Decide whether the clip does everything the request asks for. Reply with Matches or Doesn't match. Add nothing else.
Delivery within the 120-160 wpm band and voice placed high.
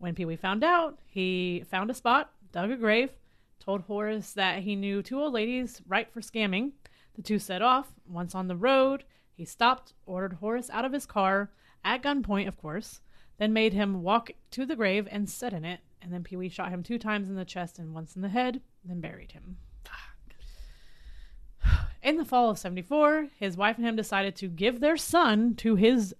Doesn't match